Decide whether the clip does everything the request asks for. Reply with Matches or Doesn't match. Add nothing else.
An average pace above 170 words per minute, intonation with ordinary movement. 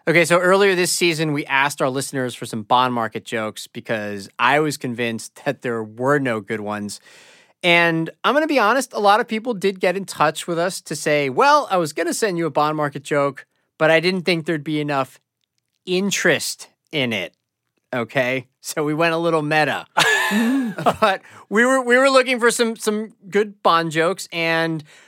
Doesn't match